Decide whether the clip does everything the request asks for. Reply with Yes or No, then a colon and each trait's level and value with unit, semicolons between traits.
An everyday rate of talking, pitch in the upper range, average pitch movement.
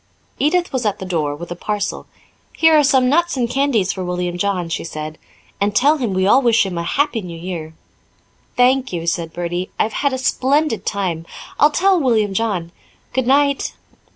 No: average, 185 wpm; high, 210 Hz; wide, 7.4 semitones